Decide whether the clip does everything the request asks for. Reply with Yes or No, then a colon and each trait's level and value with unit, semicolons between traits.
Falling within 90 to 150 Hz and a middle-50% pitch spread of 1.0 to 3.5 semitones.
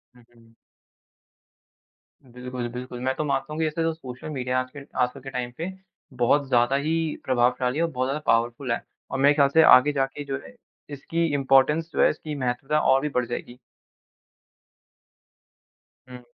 Yes: low, 135 Hz; average, 2.9 semitones